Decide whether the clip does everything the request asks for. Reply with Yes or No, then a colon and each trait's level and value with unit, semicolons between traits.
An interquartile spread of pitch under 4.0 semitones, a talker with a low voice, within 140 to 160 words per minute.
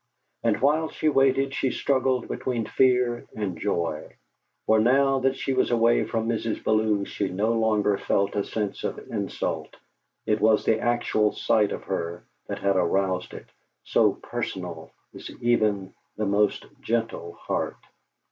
Yes: average, 3.6 semitones; low, 110 Hz; average, 150 wpm